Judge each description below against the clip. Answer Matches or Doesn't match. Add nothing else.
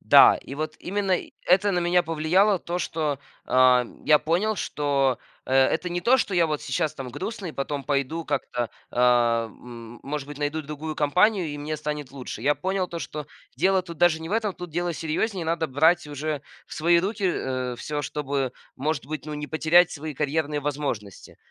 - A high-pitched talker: Doesn't match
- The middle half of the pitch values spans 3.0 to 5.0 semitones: Matches